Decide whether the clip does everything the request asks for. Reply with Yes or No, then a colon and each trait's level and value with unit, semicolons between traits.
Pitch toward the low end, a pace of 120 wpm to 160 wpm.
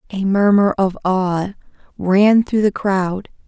No: high, 195 Hz; average, 140 wpm